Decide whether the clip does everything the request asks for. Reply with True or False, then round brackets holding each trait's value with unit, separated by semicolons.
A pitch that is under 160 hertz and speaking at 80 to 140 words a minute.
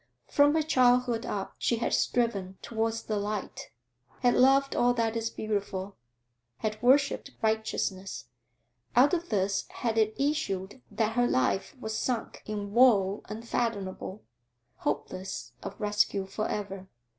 False (220 Hz; 135 wpm)